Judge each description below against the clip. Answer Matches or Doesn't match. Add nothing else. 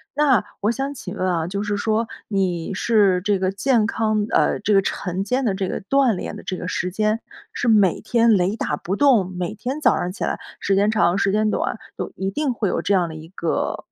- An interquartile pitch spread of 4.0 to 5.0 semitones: Doesn't match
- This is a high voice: Matches